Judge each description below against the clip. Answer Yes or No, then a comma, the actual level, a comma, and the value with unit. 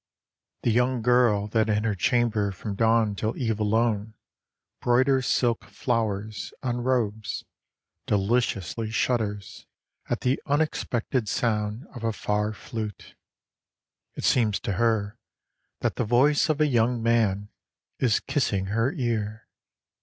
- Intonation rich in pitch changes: No, narrow, 2.6 semitones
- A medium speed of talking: No, slow, 125 wpm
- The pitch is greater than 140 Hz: No, low, 115 Hz